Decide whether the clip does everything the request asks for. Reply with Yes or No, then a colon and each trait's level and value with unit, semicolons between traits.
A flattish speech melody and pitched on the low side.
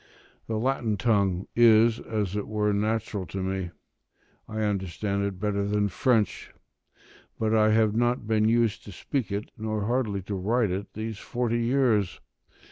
Yes: narrow, 2.1 semitones; low, 110 Hz